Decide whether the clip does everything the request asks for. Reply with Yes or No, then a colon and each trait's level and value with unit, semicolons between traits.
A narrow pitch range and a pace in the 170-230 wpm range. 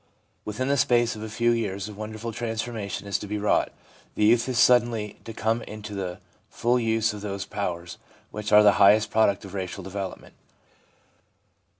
Yes: narrow, 2.3 semitones; average, 180 wpm